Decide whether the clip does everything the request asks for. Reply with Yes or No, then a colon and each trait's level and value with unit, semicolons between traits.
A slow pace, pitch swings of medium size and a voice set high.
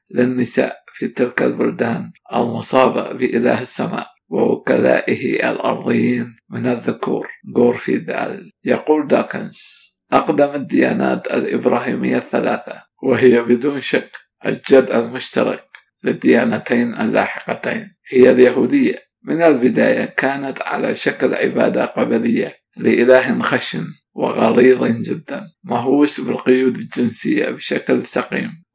No: slow, 90 wpm; average, 3.0 semitones; low, 130 Hz